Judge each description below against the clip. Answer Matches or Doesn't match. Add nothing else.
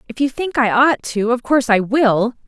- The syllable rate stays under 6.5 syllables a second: Matches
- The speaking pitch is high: Matches